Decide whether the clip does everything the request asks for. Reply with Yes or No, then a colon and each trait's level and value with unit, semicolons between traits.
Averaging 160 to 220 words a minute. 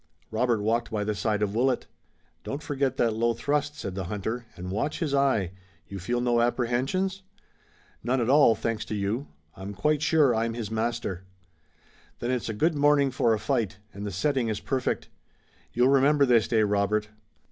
Yes: average, 180 wpm